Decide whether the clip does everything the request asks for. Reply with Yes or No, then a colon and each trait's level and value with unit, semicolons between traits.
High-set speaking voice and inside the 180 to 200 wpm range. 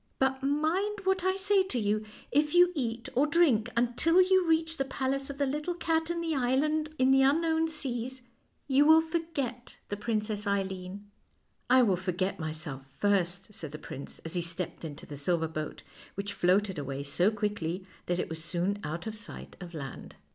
Yes: high, 235 Hz; average, 190 wpm